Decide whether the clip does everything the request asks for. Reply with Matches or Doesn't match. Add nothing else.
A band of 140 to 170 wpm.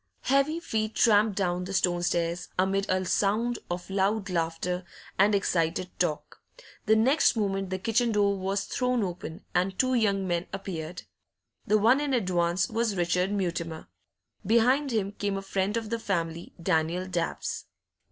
Matches